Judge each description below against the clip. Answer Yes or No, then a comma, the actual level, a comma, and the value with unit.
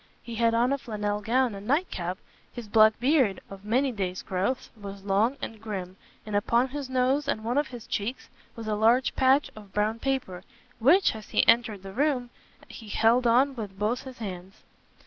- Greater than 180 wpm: Yes, average, 195 wpm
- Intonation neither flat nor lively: Yes, average, 3.8 semitones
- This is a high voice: Yes, high, 225 Hz